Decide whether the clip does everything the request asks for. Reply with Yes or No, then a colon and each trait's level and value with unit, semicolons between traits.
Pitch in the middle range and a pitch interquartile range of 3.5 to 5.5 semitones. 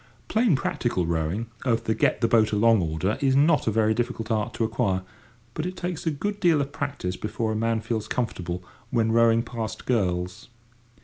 No: low, 115 Hz; average, 4.0 semitones